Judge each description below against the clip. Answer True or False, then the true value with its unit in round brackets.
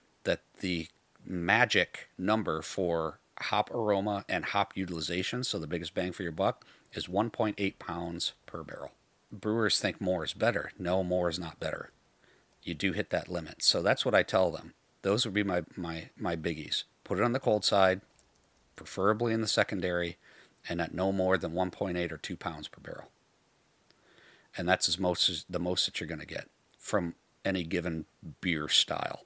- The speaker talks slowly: False (185 wpm)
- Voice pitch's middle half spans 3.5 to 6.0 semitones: False (2.6 semitones)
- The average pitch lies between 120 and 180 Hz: False (95 Hz)